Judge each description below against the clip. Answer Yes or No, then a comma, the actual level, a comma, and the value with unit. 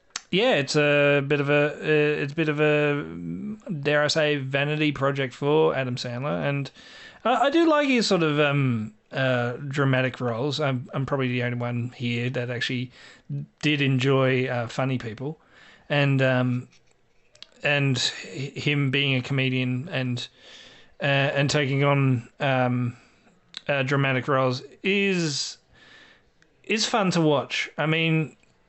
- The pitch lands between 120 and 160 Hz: Yes, medium, 140 Hz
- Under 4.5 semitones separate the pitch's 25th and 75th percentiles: Yes, average, 2.7 semitones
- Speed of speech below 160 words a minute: Yes, average, 140 wpm